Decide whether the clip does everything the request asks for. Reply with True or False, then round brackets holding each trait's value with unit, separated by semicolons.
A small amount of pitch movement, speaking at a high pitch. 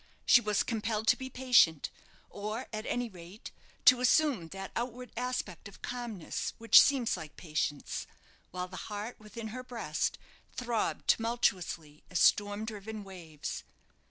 False (4.8 semitones; 215 Hz)